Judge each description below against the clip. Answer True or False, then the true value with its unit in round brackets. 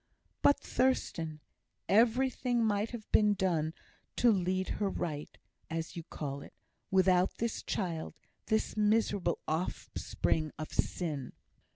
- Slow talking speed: True (115 wpm)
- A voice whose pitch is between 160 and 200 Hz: True (185 Hz)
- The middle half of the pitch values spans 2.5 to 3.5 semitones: False (5.1 semitones)